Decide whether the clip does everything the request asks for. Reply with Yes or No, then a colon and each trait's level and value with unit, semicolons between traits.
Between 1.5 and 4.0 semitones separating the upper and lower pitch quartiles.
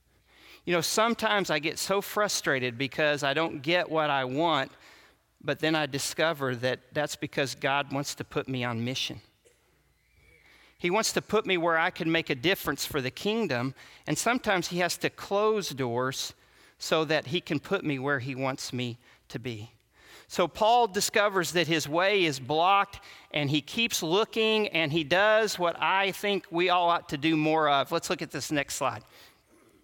No: average, 4.9 semitones